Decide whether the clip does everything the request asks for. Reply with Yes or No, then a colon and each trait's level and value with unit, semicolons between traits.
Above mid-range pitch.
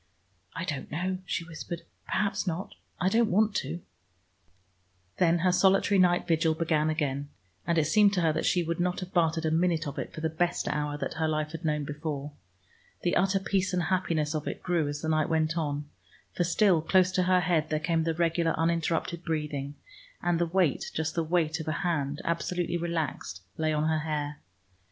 No: medium, 165 Hz